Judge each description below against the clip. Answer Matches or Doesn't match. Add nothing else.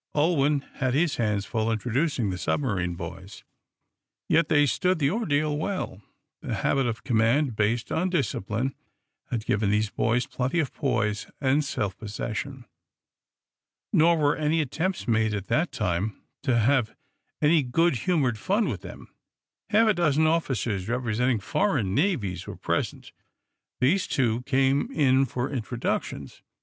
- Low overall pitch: Matches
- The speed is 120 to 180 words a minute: Matches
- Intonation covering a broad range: Matches